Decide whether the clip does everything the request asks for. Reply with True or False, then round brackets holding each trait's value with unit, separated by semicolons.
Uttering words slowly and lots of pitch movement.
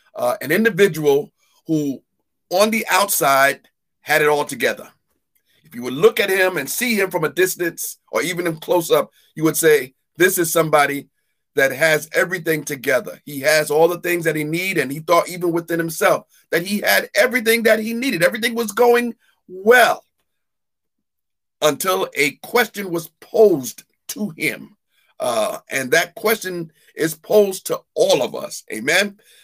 False (165 wpm; 5.7 semitones)